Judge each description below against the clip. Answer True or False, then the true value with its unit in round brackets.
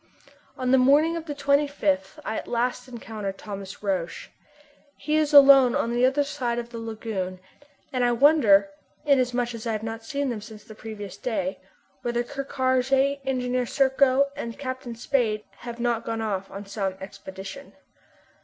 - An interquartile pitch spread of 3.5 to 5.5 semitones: True (4.0 semitones)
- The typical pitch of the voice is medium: False (240 Hz)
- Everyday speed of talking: True (165 wpm)